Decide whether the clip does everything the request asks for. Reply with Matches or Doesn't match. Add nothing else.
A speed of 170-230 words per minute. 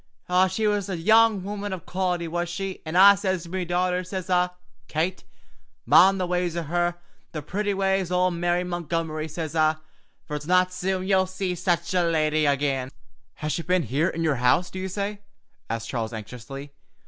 Matches